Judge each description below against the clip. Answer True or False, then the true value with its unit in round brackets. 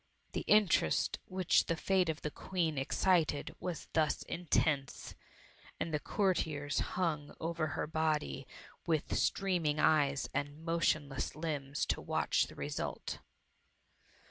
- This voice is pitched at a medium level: True (155 Hz)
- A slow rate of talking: True (120 wpm)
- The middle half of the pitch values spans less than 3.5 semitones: True (2.7 semitones)